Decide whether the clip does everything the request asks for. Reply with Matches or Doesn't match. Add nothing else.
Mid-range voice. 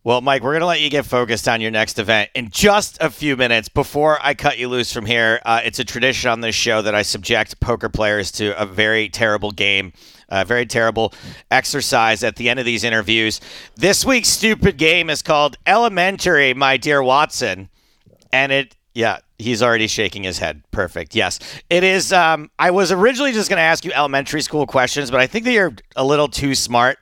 Doesn't match